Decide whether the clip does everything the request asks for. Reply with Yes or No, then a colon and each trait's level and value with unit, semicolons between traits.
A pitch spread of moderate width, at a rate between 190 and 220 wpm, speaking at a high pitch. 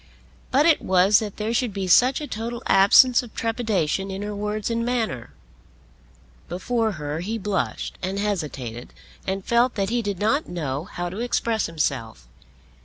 No: average, 4.7 semitones; average, 165 wpm; high, 205 Hz